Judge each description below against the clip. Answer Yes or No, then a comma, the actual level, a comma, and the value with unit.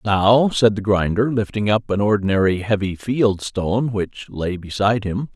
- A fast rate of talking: No, average, 170 wpm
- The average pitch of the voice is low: Yes, low, 105 Hz